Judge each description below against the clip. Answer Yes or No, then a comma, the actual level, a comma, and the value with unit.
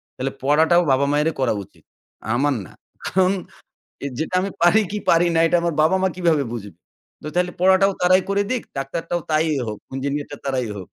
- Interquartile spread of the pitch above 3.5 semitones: Yes, average, 4.8 semitones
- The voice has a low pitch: No, medium, 160 Hz